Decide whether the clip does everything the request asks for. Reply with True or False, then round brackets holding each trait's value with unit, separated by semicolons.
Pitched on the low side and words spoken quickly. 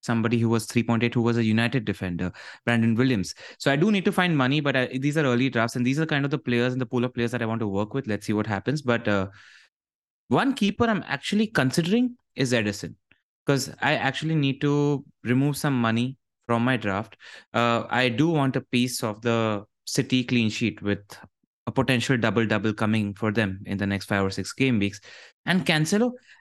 True (120 Hz; 215 wpm)